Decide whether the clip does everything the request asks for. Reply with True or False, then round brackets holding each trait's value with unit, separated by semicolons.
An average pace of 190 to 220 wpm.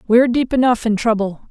True (200 wpm)